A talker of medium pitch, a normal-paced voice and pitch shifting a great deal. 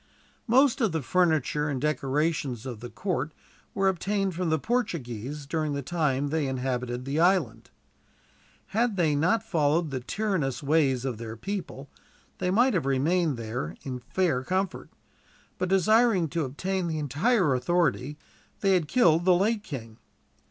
Yes: medium, 155 Hz; average, 155 wpm; wide, 5.8 semitones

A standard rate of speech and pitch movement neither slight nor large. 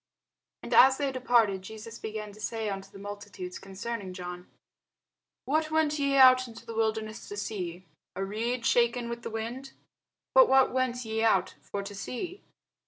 Yes: average, 170 wpm; average, 4.0 semitones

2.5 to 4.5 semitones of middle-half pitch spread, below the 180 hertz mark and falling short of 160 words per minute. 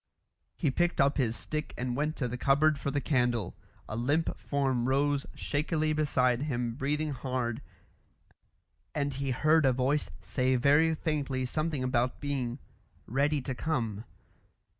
Yes: average, 2.9 semitones; medium, 140 Hz; average, 145 wpm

